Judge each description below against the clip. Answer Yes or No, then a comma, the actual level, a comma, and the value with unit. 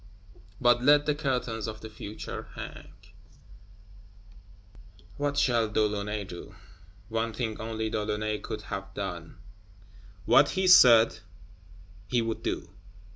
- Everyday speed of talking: No, slow, 125 wpm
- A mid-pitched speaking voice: No, low, 110 Hz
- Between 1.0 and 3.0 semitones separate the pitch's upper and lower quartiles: Yes, average, 2.7 semitones